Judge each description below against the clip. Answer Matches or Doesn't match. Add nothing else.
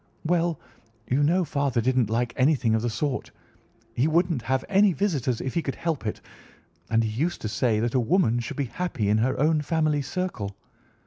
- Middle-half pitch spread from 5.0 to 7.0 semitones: Matches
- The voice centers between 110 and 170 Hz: Matches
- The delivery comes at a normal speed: Matches